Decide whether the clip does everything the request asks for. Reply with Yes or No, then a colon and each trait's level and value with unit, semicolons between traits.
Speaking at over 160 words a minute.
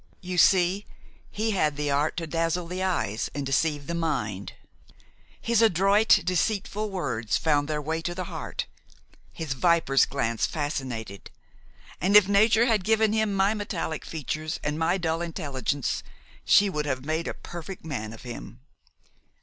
No: average, 155 wpm